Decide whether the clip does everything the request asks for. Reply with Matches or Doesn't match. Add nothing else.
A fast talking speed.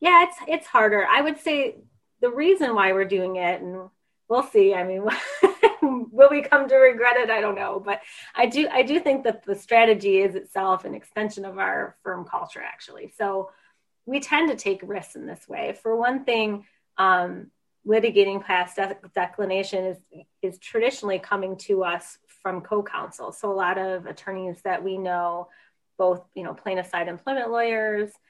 Doesn't match